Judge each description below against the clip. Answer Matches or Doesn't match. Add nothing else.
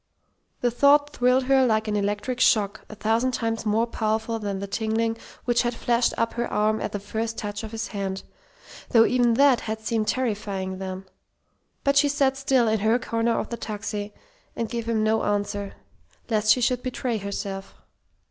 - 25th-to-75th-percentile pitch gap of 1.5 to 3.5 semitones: Matches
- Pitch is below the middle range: Doesn't match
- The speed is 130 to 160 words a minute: Doesn't match